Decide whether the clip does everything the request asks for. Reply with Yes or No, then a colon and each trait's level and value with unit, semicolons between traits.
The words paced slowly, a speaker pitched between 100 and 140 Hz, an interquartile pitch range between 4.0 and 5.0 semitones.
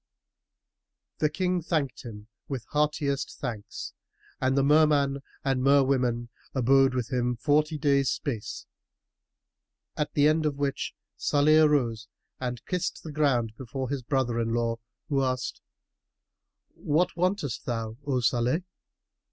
No: slow, 125 wpm; low, 135 Hz; average, 3.5 semitones